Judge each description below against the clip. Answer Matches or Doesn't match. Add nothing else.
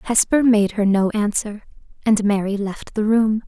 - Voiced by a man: Doesn't match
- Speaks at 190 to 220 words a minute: Doesn't match